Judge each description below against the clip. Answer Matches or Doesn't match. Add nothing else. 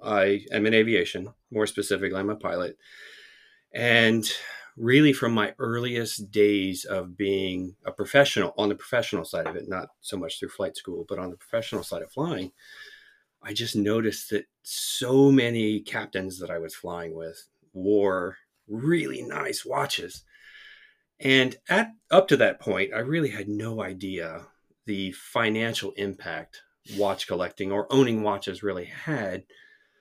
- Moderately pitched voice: Doesn't match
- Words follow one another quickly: Doesn't match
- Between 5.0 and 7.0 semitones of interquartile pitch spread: Matches